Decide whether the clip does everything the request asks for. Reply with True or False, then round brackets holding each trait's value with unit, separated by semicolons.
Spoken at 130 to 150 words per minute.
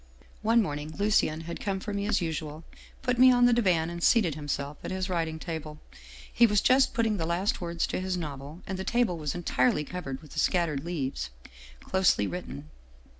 False (205 wpm)